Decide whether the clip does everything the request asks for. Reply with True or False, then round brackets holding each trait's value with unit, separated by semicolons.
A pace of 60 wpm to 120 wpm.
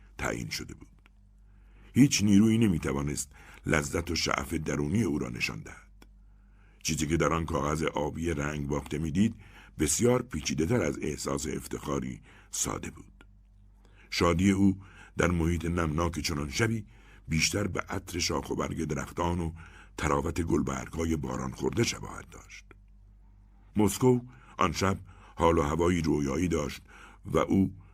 False (135 wpm)